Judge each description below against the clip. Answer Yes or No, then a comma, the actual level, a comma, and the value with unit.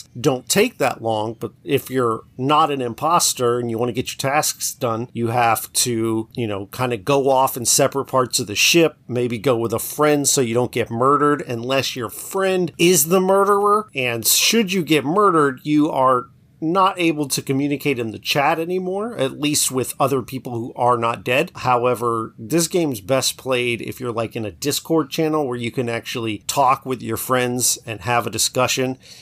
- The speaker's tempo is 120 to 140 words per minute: No, average, 200 wpm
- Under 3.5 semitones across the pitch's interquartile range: No, average, 3.8 semitones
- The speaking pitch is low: Yes, low, 130 Hz